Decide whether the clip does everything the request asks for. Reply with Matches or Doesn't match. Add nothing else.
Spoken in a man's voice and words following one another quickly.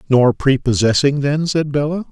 Doesn't match